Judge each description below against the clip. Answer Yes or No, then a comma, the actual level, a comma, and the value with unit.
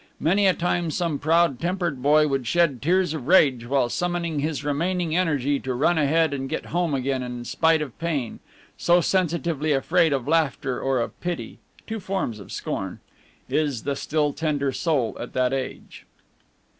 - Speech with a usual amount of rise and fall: Yes, average, 4.1 semitones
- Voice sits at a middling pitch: Yes, medium, 150 Hz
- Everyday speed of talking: Yes, average, 170 wpm